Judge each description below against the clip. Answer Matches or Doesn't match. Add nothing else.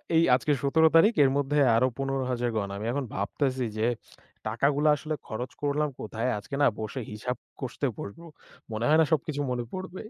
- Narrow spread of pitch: Doesn't match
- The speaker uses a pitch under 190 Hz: Matches